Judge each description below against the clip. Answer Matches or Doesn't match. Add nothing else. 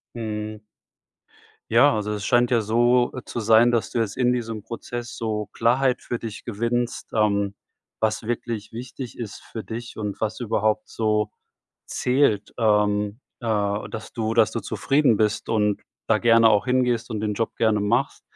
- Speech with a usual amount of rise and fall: Doesn't match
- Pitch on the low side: Matches